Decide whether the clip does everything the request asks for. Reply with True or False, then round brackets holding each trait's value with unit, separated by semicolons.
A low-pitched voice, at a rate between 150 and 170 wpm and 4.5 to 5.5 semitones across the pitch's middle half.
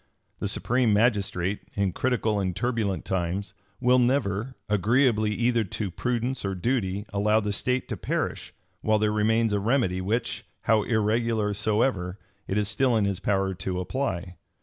False (105 Hz; 155 wpm; 3.3 semitones)